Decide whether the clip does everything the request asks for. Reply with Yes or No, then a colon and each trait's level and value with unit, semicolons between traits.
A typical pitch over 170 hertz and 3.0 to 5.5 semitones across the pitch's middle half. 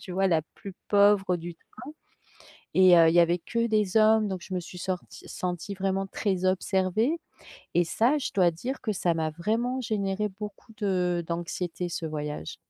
Yes: high, 190 Hz; average, 3.3 semitones